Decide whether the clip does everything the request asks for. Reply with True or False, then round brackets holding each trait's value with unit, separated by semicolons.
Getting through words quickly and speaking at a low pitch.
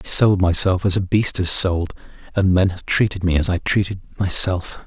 True (210 wpm; 95 Hz)